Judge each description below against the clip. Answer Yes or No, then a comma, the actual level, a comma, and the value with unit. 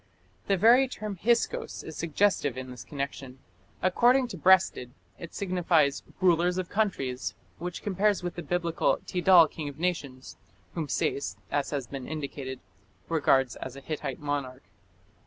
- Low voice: No, medium, 165 Hz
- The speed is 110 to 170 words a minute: Yes, average, 145 wpm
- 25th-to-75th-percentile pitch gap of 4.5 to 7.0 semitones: Yes, average, 5.2 semitones